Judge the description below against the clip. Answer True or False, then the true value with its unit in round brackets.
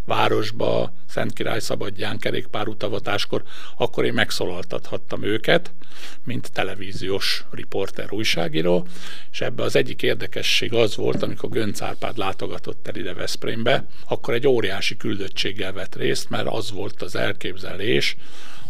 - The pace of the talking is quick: False (125 wpm)